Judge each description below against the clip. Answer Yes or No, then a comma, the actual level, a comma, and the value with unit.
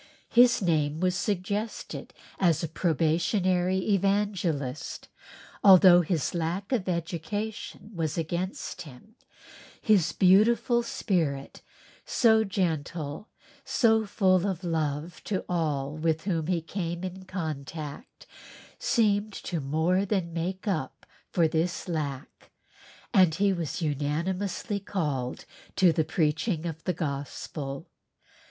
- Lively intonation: No, average, 3.9 semitones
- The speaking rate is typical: No, slow, 115 wpm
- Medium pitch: Yes, medium, 175 Hz